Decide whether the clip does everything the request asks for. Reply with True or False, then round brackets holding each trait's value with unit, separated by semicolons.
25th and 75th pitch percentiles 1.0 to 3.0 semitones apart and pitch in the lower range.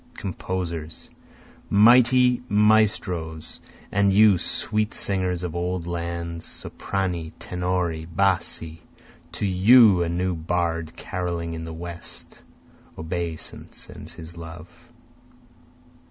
True (2.7 semitones; 90 Hz)